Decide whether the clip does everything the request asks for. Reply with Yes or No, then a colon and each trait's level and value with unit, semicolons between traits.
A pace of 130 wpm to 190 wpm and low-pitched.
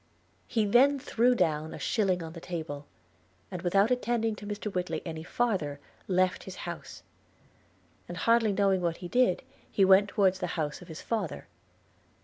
No: average, 165 wpm; high, 190 Hz